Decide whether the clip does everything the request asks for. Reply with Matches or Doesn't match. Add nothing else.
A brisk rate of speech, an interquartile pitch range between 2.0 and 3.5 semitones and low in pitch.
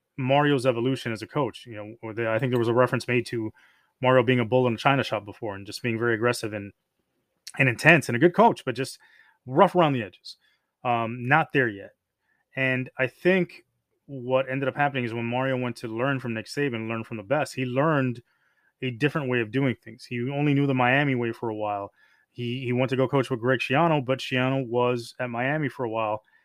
Matches